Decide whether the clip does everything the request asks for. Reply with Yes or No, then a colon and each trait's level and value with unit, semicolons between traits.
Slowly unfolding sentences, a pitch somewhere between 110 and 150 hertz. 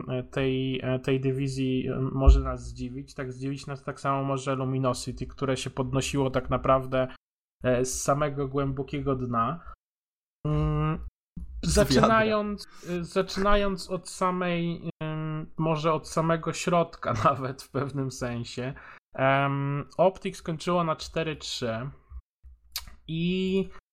Yes: slow, 100 wpm; medium, 140 Hz